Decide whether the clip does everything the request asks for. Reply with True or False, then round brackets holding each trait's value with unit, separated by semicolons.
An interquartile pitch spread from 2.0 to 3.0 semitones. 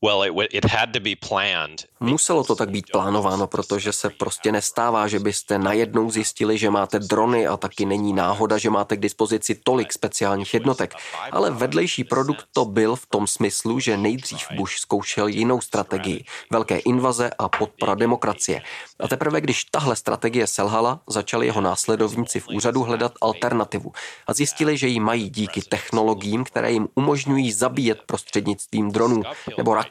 True (2.5 semitones)